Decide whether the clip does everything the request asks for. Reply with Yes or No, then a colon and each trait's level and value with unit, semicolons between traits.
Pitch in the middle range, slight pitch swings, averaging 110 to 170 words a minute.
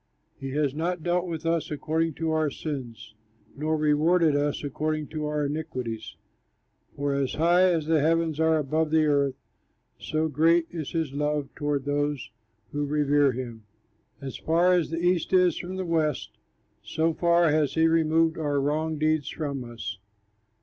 Yes: medium, 155 Hz; narrow, 2.2 semitones; average, 165 wpm